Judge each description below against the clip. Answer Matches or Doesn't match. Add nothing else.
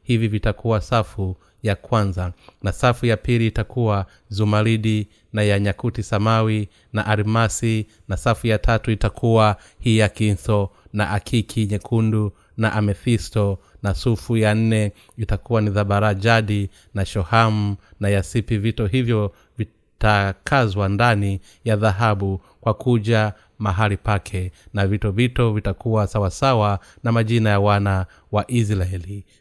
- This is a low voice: Matches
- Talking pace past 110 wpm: Matches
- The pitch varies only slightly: Matches